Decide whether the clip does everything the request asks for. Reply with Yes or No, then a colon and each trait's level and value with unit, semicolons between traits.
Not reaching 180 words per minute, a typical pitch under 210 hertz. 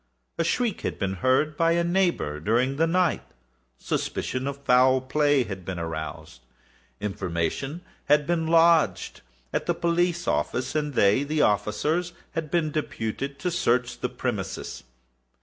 Yes: average, 145 wpm; medium, 140 Hz